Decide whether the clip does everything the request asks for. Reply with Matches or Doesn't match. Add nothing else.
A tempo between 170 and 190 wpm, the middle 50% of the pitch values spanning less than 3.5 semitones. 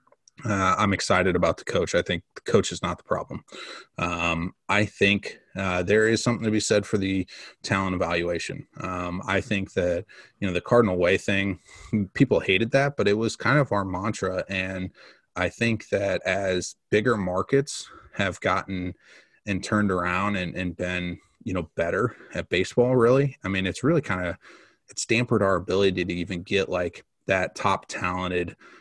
Matches